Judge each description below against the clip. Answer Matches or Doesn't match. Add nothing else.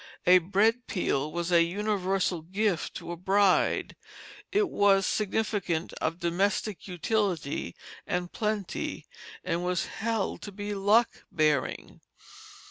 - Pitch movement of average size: Matches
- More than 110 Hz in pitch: Matches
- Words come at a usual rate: Doesn't match